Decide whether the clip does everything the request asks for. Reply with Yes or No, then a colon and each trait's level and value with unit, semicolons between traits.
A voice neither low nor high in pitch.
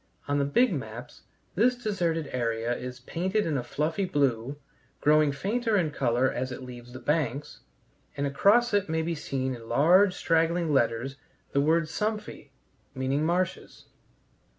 Yes: medium, 150 Hz